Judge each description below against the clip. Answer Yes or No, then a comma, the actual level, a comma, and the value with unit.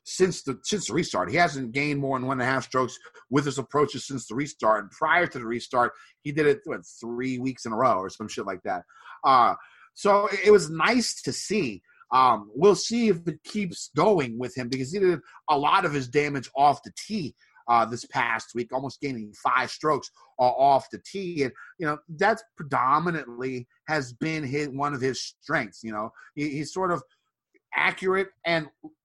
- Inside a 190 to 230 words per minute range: Yes, average, 200 wpm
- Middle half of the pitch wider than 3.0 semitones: Yes, wide, 5.4 semitones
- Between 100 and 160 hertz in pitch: Yes, medium, 140 Hz